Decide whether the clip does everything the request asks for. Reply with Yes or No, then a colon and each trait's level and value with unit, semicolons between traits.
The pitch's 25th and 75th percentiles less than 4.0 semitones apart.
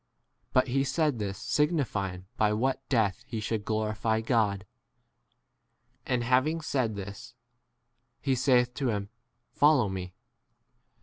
No: average, 4.3 semitones